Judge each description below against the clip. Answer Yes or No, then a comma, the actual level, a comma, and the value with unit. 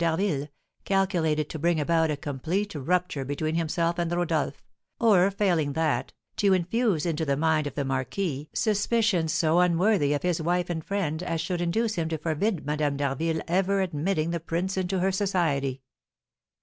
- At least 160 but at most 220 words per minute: Yes, average, 165 wpm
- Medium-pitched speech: Yes, medium, 165 Hz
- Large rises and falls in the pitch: No, average, 3.6 semitones